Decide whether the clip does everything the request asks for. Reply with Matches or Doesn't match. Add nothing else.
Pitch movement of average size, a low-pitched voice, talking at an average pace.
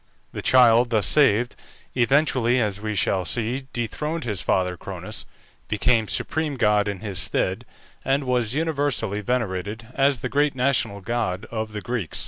Matches